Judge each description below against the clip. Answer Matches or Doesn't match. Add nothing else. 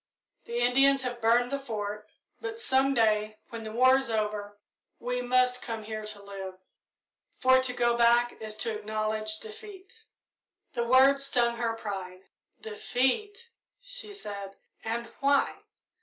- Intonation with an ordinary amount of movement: Matches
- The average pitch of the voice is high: Matches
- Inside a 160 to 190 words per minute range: Doesn't match